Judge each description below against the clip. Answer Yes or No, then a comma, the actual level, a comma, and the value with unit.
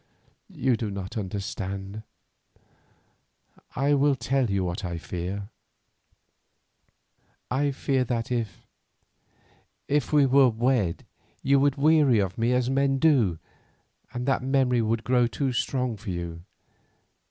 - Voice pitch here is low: Yes, low, 120 Hz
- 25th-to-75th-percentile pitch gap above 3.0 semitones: Yes, average, 5.3 semitones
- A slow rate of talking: Yes, slow, 120 wpm